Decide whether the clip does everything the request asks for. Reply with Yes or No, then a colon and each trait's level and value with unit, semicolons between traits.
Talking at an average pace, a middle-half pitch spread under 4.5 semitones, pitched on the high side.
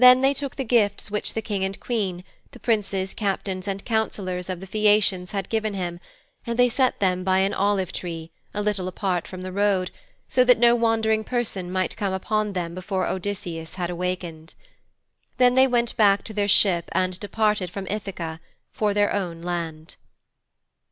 Yes: average, 180 wpm; average, 2.9 semitones; high, 195 Hz